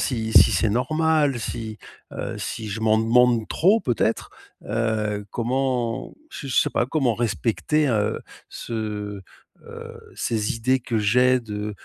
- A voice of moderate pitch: No, low, 115 Hz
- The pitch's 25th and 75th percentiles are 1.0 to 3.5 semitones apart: Yes, average, 2.8 semitones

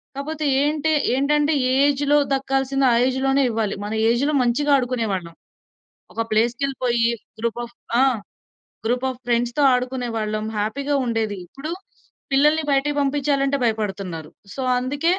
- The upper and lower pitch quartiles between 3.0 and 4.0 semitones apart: Yes, average, 3.6 semitones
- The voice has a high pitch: Yes, very high, 260 Hz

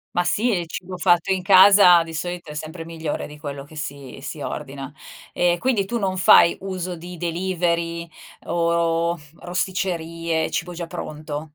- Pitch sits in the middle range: Yes, medium, 170 Hz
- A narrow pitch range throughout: Yes, narrow, 2.0 semitones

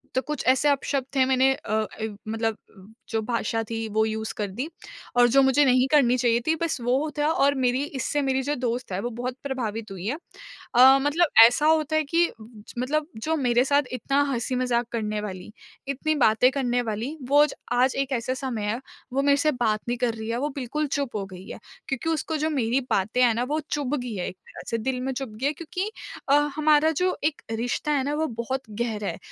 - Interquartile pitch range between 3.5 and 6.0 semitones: Yes, average, 4.0 semitones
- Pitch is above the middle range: Yes, very high, 255 Hz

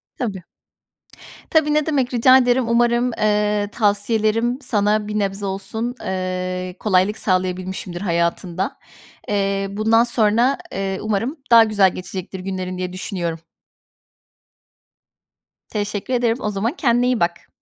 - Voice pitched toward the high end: Yes, high, 210 Hz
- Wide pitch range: No, average, 3.8 semitones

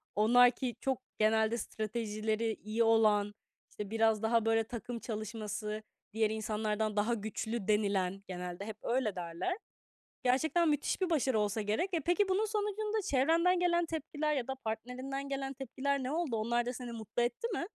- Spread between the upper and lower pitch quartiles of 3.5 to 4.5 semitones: Yes, average, 4.2 semitones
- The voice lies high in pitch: Yes, high, 230 Hz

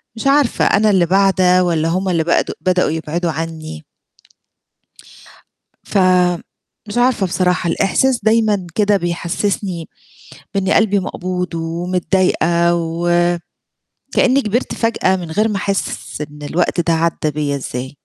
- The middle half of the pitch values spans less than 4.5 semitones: Yes, average, 3.0 semitones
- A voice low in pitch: No, medium, 180 Hz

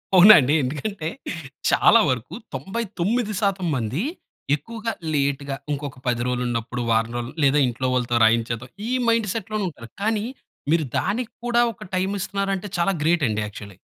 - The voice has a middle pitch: Yes, medium, 155 Hz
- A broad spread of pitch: Yes, wide, 8.6 semitones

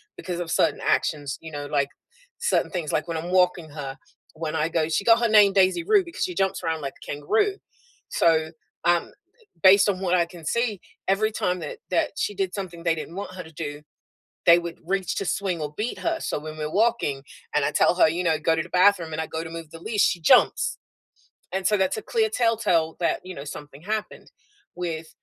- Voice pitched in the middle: Yes, medium, 175 Hz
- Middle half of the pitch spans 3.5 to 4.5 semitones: Yes, average, 4.0 semitones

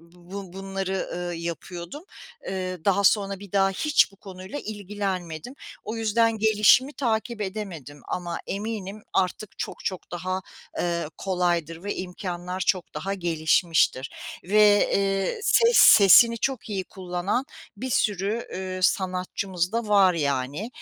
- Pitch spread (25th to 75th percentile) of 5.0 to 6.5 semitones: No, average, 2.9 semitones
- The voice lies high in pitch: Yes, high, 195 Hz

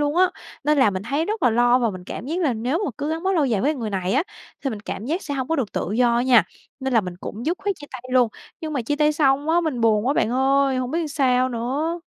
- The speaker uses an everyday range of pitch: Yes, average, 4.3 semitones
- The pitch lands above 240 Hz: Yes, very high, 265 Hz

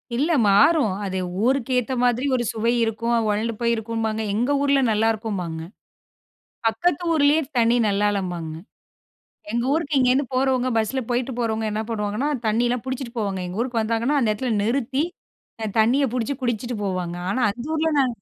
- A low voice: No, high, 235 Hz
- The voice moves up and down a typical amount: Yes, average, 3.3 semitones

